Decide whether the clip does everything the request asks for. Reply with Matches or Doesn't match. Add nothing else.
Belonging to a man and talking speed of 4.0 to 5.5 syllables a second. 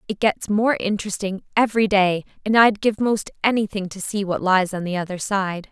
Doesn't match